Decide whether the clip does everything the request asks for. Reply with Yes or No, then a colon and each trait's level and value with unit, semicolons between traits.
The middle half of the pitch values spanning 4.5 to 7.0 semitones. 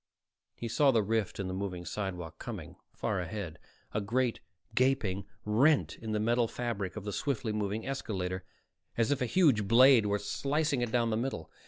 No: average, 4.1 semitones